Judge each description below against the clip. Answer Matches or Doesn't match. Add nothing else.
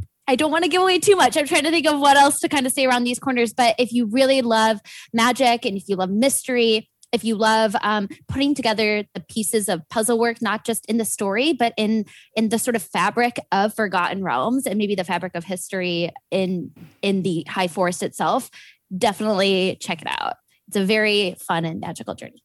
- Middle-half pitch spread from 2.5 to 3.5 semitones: Doesn't match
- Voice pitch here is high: Matches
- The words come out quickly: Matches